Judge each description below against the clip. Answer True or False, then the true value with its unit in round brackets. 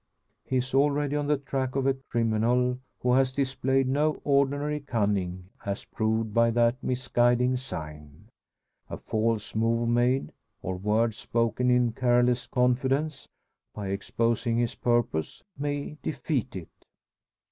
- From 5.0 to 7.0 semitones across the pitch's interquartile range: False (2.9 semitones)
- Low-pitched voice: True (125 Hz)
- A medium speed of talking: False (130 wpm)